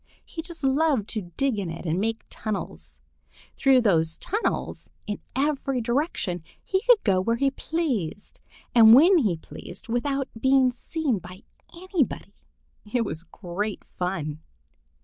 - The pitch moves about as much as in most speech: No, wide, 6.8 semitones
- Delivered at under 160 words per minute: Yes, average, 140 wpm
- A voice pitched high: Yes, high, 235 Hz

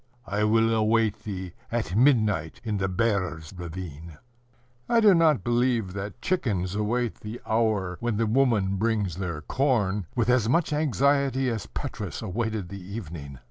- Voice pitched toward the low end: Yes, low, 110 Hz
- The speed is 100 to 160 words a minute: Yes, average, 150 wpm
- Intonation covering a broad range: No, average, 4.3 semitones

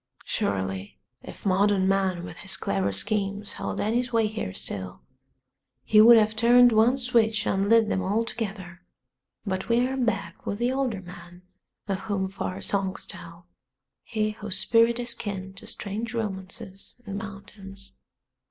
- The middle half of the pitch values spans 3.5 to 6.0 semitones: No, average, 3.1 semitones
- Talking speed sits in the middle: Yes, average, 150 wpm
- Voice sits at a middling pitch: No, high, 200 Hz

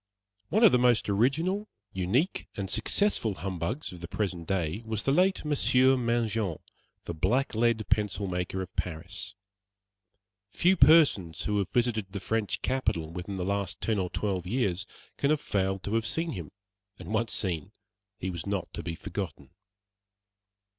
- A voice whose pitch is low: Yes, low, 105 Hz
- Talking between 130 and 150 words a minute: No, average, 160 wpm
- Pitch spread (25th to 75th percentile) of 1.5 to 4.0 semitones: No, average, 5.0 semitones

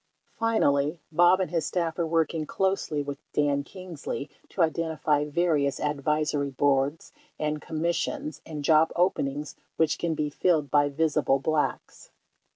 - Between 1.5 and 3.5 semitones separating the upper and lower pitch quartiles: Yes, average, 2.7 semitones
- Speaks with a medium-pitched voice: Yes, medium, 155 Hz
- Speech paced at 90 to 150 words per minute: Yes, average, 145 wpm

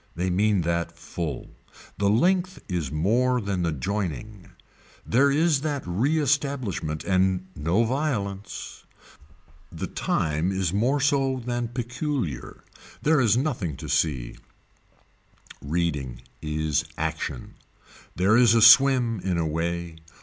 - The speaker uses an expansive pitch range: Yes, wide, 7.0 semitones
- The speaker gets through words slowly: Yes, slow, 120 wpm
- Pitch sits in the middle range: No, low, 100 Hz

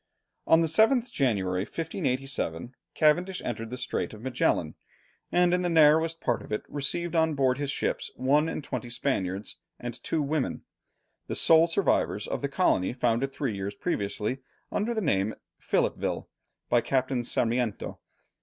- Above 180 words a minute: No, average, 155 wpm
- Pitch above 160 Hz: No, low, 135 Hz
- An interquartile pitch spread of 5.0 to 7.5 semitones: Yes, wide, 5.5 semitones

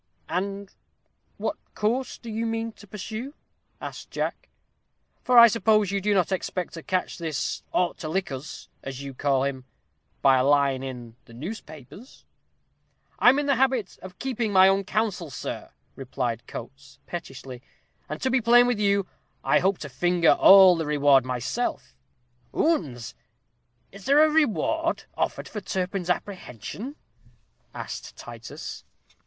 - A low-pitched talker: No, medium, 185 Hz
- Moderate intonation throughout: No, wide, 8.2 semitones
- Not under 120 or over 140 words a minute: No, average, 150 wpm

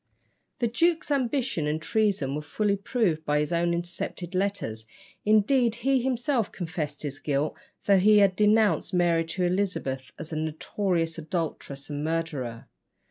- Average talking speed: Yes, average, 145 wpm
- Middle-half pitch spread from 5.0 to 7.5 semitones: Yes, wide, 5.6 semitones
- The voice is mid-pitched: Yes, medium, 175 Hz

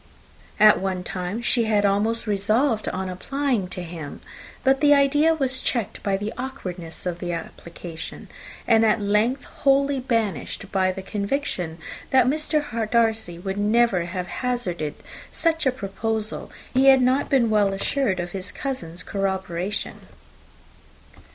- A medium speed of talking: Yes, average, 145 wpm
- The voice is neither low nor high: No, high, 215 Hz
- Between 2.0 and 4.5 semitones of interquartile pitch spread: No, wide, 5.6 semitones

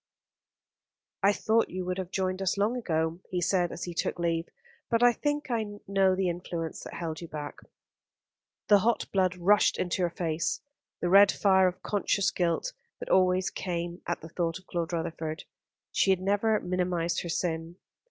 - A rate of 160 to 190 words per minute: Yes, average, 180 wpm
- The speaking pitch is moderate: Yes, medium, 180 Hz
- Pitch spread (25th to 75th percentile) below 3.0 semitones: Yes, narrow, 2.6 semitones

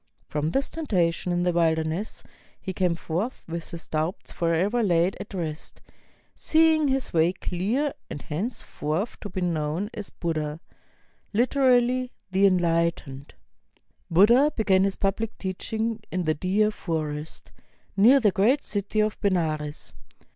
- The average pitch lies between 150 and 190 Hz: Yes, medium, 185 Hz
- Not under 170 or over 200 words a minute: No, slow, 135 wpm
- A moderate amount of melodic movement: Yes, average, 5.0 semitones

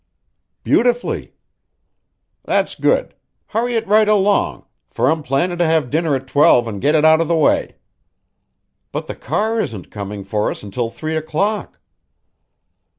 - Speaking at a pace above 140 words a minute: Yes, average, 150 wpm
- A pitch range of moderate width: No, wide, 8.6 semitones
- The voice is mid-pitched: Yes, medium, 160 Hz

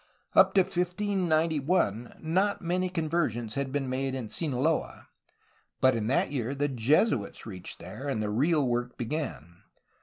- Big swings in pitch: Yes, wide, 5.8 semitones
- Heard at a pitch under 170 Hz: Yes, medium, 140 Hz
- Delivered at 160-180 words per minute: No, average, 145 wpm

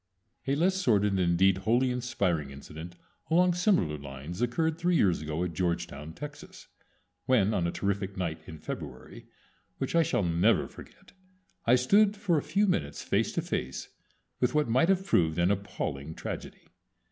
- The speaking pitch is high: No, low, 100 Hz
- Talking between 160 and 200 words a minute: Yes, average, 165 wpm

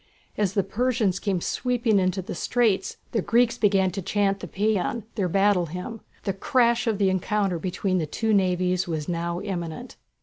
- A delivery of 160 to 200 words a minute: Yes, average, 175 wpm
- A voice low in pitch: No, high, 195 Hz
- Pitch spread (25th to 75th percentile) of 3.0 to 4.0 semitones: Yes, average, 3.3 semitones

